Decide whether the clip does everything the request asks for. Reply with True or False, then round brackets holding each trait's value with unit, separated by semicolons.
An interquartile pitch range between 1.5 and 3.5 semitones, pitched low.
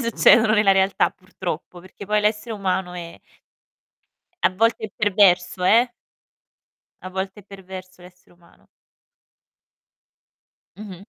False (2.5 semitones; 190 Hz)